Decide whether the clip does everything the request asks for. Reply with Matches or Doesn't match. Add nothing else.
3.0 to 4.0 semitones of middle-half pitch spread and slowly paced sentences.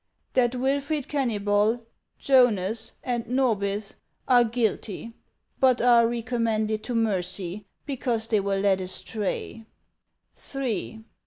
Matches